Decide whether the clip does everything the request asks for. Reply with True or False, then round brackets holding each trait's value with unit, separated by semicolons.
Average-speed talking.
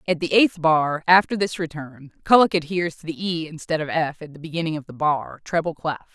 False (225 wpm)